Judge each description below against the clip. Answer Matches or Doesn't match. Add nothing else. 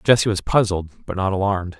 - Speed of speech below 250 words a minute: Matches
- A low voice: Matches